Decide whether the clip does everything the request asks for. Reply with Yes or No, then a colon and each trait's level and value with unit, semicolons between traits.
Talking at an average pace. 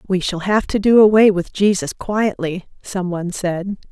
Yes: average, 170 wpm